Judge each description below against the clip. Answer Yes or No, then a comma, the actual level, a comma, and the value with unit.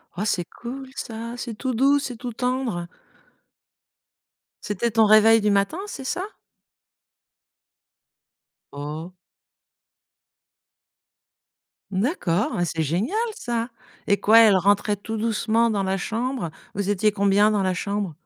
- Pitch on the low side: No, high, 215 Hz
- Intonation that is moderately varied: Yes, average, 3.3 semitones